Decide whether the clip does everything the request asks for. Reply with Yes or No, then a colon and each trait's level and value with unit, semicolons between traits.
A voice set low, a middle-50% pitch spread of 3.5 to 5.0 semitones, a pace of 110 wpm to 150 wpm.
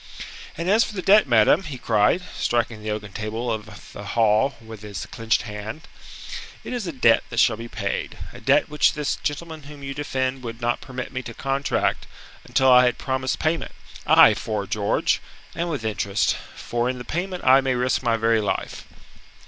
No: low, 125 Hz; average, 4.4 semitones; average, 190 wpm